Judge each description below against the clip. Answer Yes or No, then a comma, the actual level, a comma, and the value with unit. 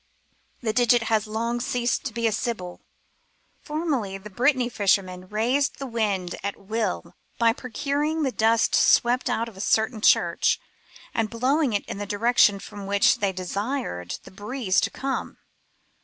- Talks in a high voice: Yes, high, 225 Hz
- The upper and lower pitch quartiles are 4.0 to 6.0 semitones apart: No, average, 3.6 semitones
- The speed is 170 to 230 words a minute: No, average, 155 wpm